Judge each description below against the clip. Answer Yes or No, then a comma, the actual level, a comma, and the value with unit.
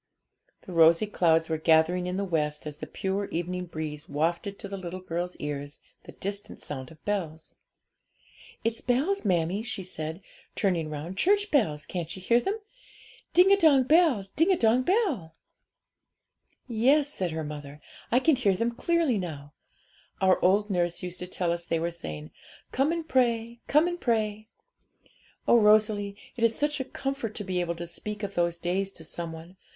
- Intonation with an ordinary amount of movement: No, wide, 6.2 semitones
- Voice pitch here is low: No, high, 190 Hz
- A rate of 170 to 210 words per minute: Yes, average, 175 wpm